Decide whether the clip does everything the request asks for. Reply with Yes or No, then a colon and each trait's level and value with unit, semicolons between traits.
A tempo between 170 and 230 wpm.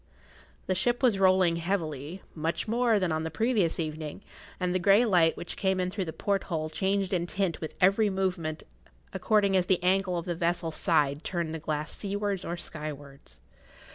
Yes: average, 180 wpm